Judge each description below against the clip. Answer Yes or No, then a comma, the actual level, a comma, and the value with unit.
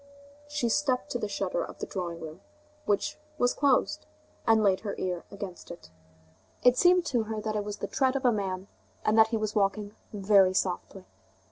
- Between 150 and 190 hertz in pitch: No, high, 210 Hz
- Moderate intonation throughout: Yes, average, 4.1 semitones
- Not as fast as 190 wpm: No, average, 195 wpm